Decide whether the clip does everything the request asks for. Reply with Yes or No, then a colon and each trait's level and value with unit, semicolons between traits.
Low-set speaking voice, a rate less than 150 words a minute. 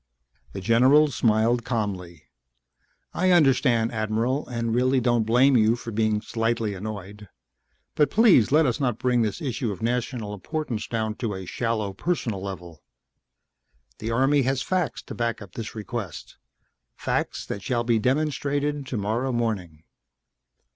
Yes: low, 115 Hz; average, 140 wpm